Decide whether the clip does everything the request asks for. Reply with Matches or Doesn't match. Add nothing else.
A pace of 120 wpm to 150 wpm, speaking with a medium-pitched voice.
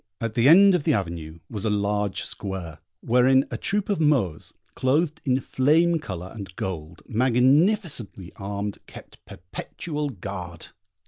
Doesn't match